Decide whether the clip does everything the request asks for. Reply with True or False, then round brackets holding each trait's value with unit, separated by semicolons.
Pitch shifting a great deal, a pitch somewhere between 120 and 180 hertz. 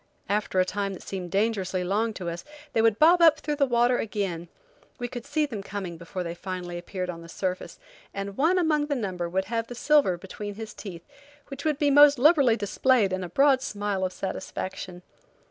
False (6.2 semitones; 205 Hz)